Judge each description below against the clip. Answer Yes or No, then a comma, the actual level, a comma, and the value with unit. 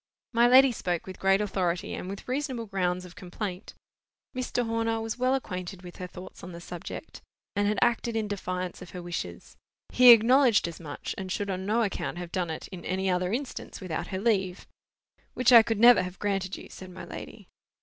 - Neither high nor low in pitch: No, high, 195 Hz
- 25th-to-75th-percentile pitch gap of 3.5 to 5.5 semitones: Yes, average, 4.0 semitones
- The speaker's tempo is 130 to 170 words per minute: No, average, 200 wpm